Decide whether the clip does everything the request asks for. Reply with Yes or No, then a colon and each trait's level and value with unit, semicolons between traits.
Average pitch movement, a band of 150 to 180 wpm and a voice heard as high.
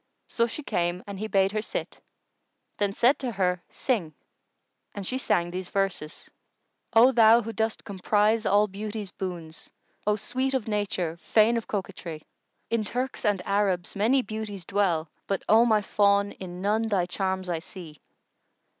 Yes: average, 3.2 semitones; average, 165 wpm; high, 205 Hz